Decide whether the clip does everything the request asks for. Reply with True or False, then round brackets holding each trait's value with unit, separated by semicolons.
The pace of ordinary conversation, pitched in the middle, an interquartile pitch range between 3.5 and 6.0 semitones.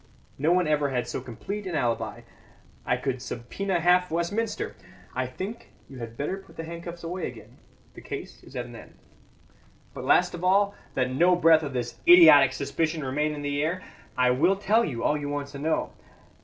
True (195 wpm; 155 Hz; 5.4 semitones)